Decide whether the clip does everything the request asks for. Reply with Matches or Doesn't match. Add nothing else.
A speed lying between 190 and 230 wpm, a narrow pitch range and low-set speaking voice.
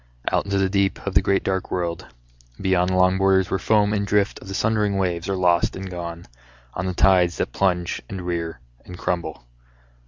Matches